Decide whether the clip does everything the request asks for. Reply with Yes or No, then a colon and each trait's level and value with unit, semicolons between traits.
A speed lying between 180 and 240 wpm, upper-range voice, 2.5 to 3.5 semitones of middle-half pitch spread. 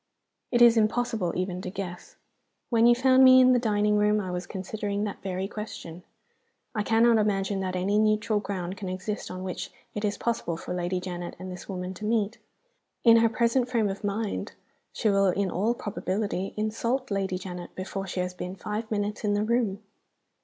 Yes: average, 190 wpm; high, 205 Hz; average, 3.1 semitones